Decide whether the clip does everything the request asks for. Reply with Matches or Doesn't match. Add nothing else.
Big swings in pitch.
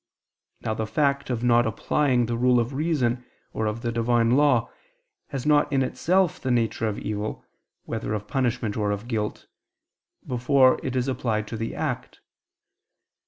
Doesn't match